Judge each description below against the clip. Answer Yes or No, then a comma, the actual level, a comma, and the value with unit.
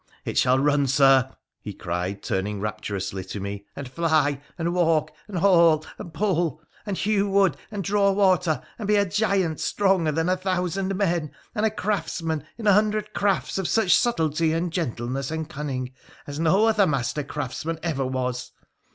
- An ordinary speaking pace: Yes, average, 175 wpm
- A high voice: No, medium, 165 Hz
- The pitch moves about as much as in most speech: No, wide, 6.3 semitones